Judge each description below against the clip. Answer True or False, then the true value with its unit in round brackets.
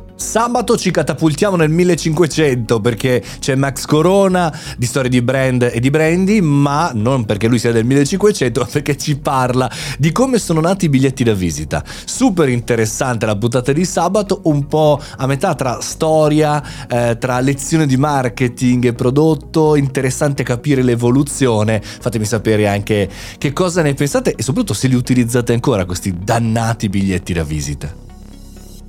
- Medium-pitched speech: False (130 Hz)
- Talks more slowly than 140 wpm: False (155 wpm)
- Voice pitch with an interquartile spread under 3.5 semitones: False (4.9 semitones)